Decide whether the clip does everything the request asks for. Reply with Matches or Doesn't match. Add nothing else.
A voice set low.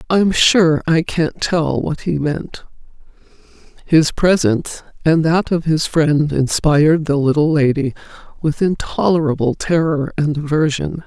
Doesn't match